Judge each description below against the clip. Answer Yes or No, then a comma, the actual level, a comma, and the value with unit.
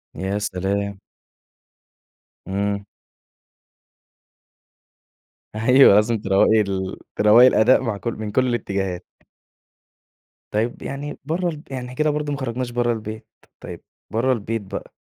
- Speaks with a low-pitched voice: Yes, low, 110 Hz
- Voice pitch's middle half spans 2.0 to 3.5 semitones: No, average, 4.1 semitones